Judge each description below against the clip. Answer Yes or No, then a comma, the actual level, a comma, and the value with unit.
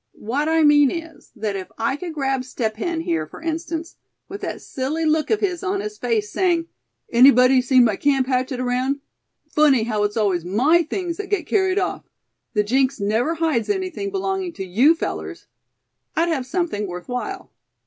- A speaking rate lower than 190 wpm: Yes, average, 180 wpm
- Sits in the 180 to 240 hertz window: No, very high, 290 Hz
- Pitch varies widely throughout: Yes, wide, 5.7 semitones